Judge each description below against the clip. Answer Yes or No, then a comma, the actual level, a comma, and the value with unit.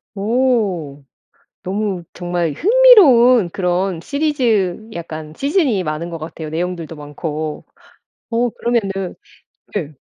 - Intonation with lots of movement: Yes, wide, 6.5 semitones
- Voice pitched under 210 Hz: Yes, high, 190 Hz